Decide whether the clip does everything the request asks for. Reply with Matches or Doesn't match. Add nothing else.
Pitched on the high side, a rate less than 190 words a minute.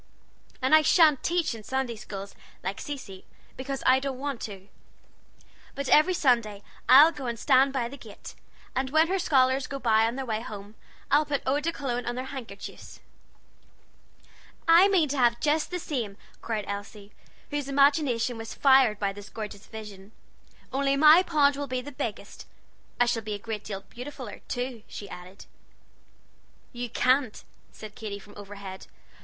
Matches